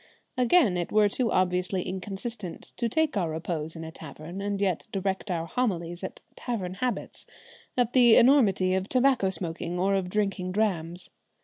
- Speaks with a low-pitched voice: No, high, 190 Hz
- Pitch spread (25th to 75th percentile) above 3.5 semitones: Yes, average, 3.9 semitones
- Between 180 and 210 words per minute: No, average, 165 wpm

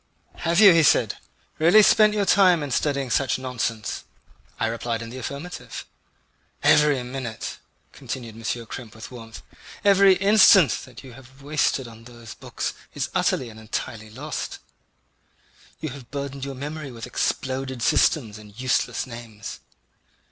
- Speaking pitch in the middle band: No, low, 130 Hz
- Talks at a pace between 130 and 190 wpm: Yes, average, 145 wpm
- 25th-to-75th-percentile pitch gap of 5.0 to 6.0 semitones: No, average, 4.5 semitones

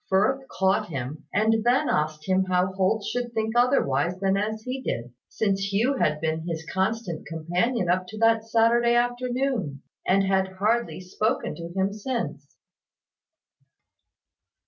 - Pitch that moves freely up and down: No, average, 4.7 semitones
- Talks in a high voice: Yes, high, 195 Hz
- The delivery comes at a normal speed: Yes, average, 145 wpm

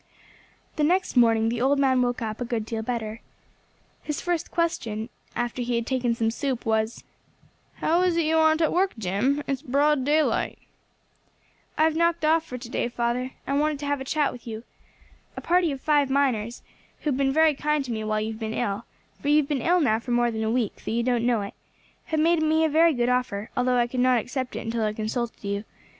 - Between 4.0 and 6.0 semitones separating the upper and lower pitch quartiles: Yes, average, 4.7 semitones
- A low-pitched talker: No, very high, 255 Hz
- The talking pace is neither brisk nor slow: No, fast, 230 wpm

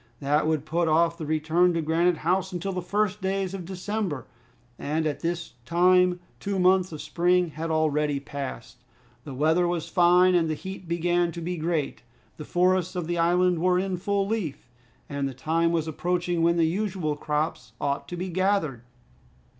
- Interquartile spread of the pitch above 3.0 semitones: No, narrow, 2.6 semitones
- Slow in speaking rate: No, average, 180 wpm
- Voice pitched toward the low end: No, medium, 170 Hz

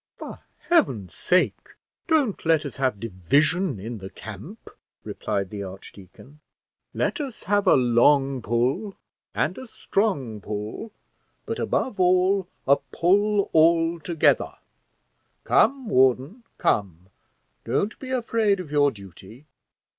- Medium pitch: Yes, medium, 150 Hz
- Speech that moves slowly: Yes, slow, 120 wpm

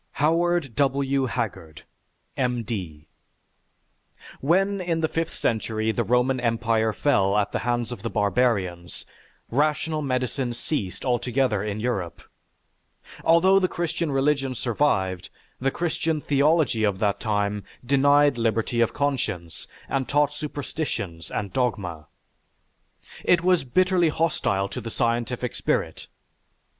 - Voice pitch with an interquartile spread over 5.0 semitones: Yes, wide, 5.4 semitones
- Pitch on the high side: No, low, 125 Hz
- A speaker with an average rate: No, slow, 120 wpm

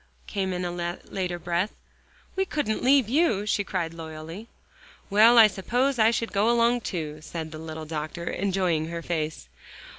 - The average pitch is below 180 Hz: No, medium, 185 Hz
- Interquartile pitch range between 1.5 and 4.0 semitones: No, wide, 5.5 semitones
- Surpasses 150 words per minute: Yes, average, 160 wpm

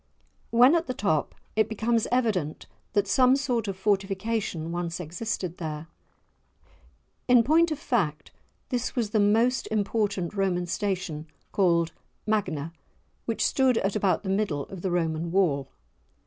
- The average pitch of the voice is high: Yes, high, 200 Hz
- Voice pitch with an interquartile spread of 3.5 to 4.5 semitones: No, average, 5.1 semitones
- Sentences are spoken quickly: No, slow, 135 wpm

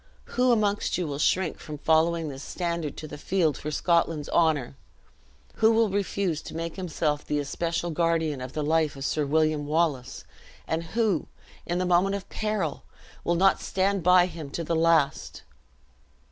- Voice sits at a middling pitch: Yes, medium, 165 Hz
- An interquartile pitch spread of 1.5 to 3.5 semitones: Yes, average, 3.1 semitones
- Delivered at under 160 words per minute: No, average, 170 wpm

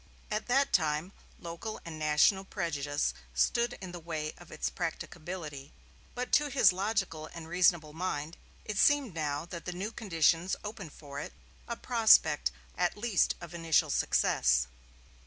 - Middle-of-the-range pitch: Yes, medium, 170 Hz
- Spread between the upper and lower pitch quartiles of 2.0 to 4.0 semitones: No, average, 5.1 semitones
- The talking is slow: No, average, 150 wpm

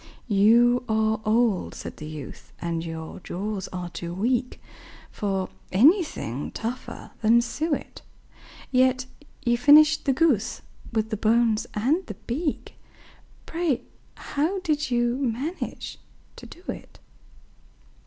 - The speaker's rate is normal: No, slow, 120 wpm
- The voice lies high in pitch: Yes, high, 235 Hz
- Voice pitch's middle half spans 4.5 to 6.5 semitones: Yes, wide, 5.4 semitones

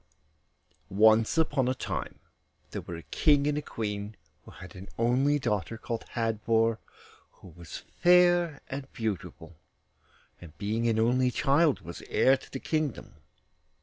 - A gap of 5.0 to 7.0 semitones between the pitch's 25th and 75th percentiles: Yes, average, 5.3 semitones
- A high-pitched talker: No, low, 115 Hz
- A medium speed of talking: Yes, average, 145 wpm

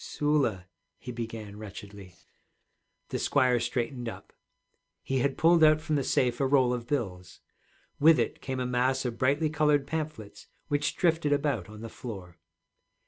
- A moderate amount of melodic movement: Yes, average, 4.5 semitones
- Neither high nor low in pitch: No, low, 130 Hz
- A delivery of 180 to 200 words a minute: No, average, 155 wpm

